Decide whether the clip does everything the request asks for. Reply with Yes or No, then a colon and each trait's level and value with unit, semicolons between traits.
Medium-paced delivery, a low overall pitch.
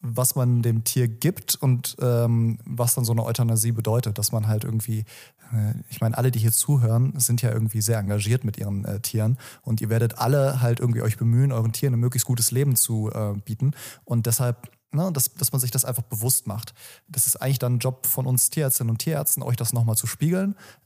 No: fast, 220 wpm; low, 120 Hz